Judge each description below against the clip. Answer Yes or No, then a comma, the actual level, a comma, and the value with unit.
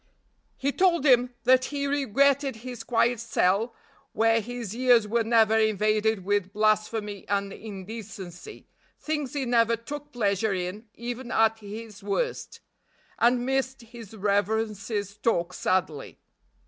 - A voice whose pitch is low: No, high, 225 Hz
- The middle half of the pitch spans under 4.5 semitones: Yes, average, 3.3 semitones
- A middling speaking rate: No, slow, 125 wpm